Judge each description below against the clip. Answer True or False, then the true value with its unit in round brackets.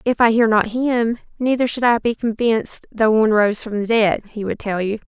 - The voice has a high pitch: True (225 Hz)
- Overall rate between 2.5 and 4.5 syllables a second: False (5.2 syllables/s)